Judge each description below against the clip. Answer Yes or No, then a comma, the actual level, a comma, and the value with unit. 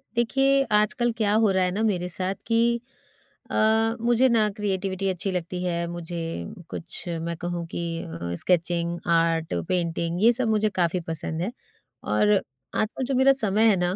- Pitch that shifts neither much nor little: Yes, average, 4.6 semitones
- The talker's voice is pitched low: No, medium, 185 Hz